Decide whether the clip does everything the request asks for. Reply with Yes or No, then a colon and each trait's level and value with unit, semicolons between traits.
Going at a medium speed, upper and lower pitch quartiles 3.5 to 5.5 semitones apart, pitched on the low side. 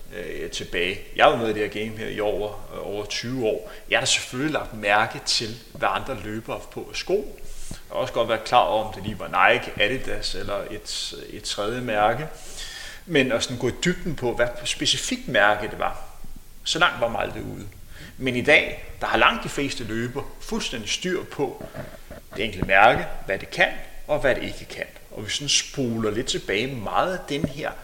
Yes: average, 205 wpm; average, 4.5 semitones; low, 120 Hz